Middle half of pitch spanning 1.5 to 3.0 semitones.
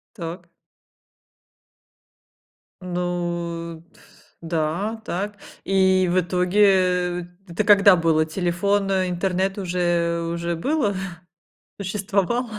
Yes: narrow, 2.5 semitones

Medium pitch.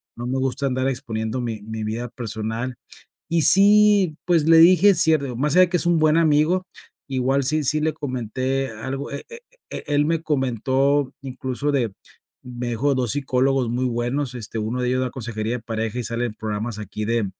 No: low, 130 Hz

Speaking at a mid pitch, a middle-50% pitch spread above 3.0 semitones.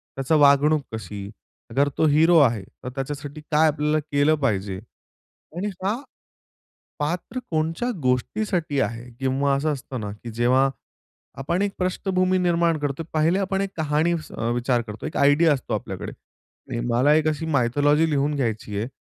Yes: medium, 145 Hz; average, 4.1 semitones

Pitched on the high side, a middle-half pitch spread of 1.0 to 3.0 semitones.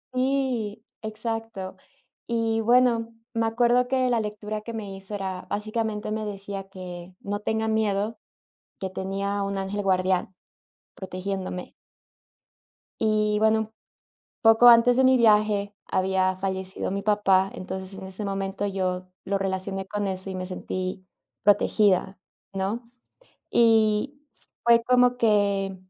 Yes: high, 205 Hz; average, 2.7 semitones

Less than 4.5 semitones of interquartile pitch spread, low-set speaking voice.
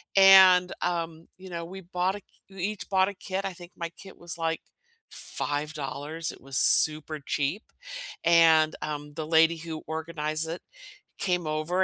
No: average, 2.9 semitones; medium, 165 Hz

